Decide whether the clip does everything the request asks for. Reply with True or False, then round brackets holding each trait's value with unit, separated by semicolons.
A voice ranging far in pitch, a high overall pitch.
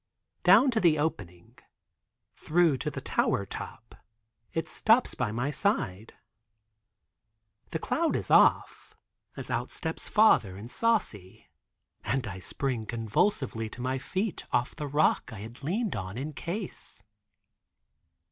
False (8.4 semitones; 135 Hz)